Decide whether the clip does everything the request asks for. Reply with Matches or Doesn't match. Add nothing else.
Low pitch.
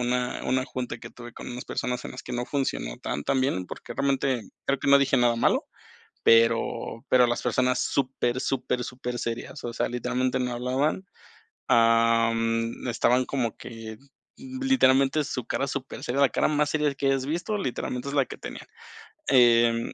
Matches